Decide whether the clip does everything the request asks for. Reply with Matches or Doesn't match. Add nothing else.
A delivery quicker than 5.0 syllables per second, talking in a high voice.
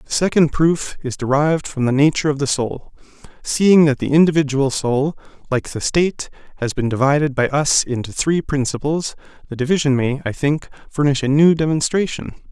Doesn't match